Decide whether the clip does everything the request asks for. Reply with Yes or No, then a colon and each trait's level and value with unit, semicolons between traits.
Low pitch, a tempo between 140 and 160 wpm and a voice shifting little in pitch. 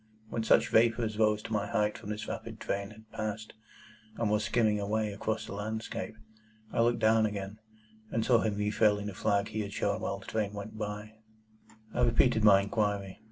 No: low, 105 Hz; average, 200 wpm; narrow, 1.3 semitones